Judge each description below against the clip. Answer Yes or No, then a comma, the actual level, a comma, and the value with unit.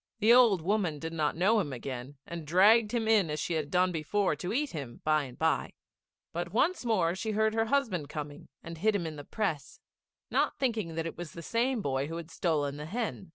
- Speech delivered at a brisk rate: Yes, fast, 225 wpm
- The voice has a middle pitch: Yes, medium, 175 Hz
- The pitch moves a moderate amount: No, wide, 6.1 semitones